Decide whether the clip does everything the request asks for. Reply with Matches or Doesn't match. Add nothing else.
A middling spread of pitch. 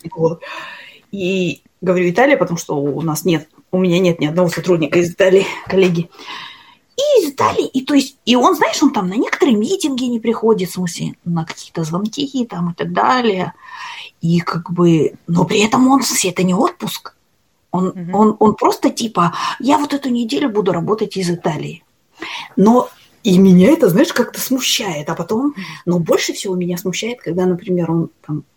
Doesn't match